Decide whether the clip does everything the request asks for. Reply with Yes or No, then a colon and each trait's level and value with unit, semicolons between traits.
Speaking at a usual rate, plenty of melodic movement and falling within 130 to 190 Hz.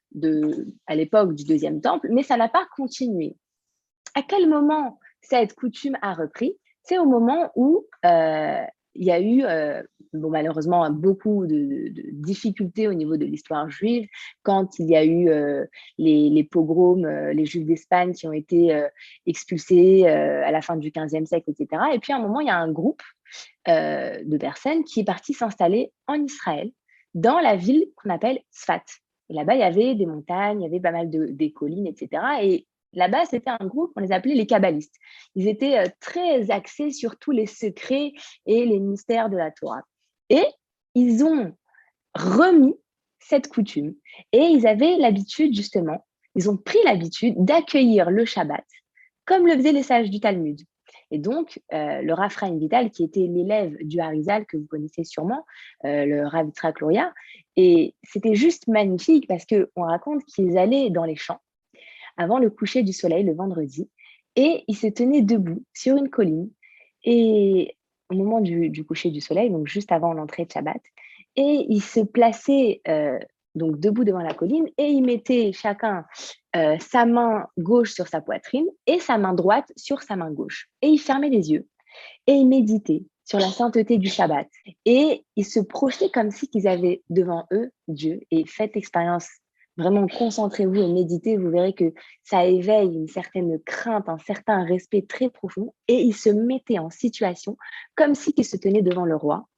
No: average, 180 wpm; wide, 7.3 semitones; high, 210 Hz